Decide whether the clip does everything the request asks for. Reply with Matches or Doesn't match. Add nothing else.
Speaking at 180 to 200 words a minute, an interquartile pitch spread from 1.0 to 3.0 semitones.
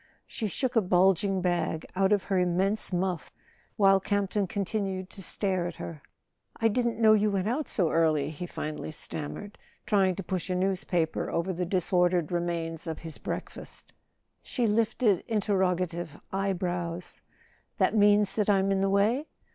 Doesn't match